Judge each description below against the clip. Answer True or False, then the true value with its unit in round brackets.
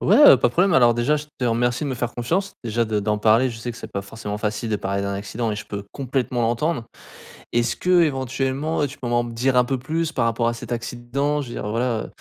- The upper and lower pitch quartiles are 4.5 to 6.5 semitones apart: False (2.8 semitones)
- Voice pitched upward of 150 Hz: False (120 Hz)